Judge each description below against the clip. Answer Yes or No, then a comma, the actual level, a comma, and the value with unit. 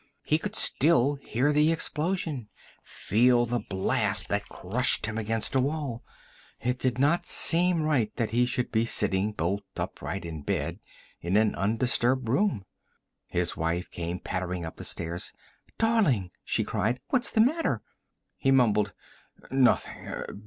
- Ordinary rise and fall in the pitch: No, wide, 6.3 semitones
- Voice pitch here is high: No, low, 120 Hz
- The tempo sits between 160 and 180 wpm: No, average, 145 wpm